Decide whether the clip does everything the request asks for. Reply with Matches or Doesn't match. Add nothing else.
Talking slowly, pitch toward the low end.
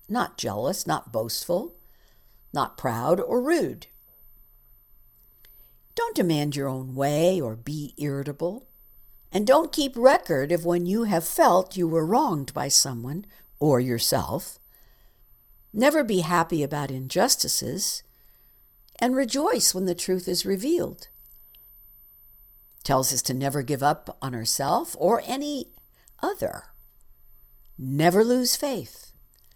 Doesn't match